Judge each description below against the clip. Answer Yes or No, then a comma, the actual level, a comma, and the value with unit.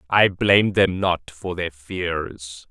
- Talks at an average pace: Yes, average, 155 wpm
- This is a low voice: Yes, very low, 90 Hz